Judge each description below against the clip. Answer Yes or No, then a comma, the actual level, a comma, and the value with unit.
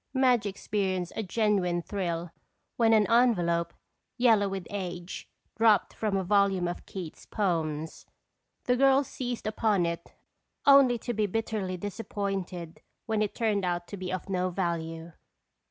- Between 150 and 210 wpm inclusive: No, average, 140 wpm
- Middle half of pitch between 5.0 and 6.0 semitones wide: No, average, 4.0 semitones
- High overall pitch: Yes, high, 195 Hz